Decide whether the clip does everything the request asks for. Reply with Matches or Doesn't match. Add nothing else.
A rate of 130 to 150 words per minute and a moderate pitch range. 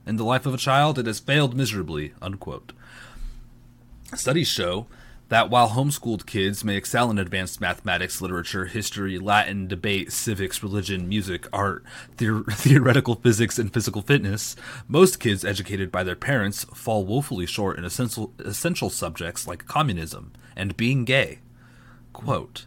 Matches